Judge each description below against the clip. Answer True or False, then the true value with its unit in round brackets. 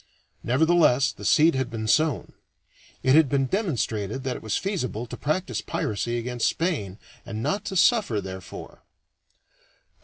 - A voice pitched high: False (130 Hz)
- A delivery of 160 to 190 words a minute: False (145 wpm)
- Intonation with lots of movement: True (6.3 semitones)